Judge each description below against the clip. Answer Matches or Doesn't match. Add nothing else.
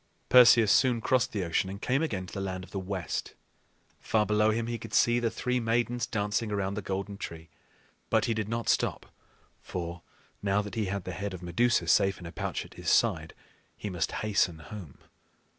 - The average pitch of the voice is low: Matches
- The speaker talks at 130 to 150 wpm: Doesn't match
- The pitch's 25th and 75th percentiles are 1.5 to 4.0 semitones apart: Matches